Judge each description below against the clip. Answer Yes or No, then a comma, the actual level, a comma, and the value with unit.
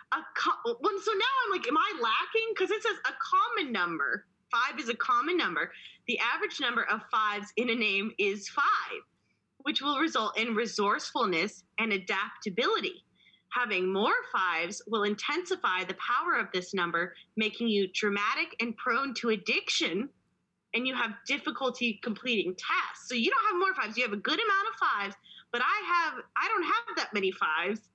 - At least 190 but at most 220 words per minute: No, average, 180 wpm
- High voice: Yes, high, 235 Hz